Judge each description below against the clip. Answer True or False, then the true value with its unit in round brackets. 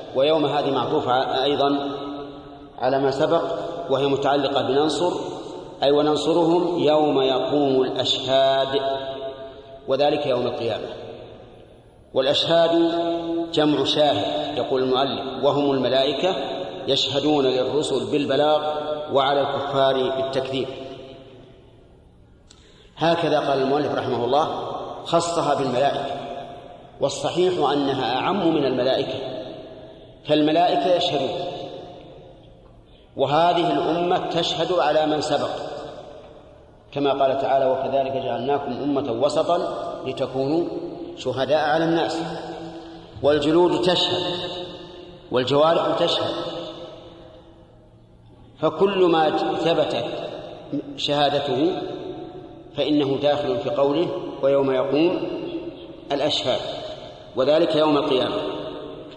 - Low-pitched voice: False (145 Hz)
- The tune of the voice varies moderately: True (3.6 semitones)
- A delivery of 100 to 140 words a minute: False (80 wpm)